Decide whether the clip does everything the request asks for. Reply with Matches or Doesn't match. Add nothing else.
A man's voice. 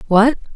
Doesn't match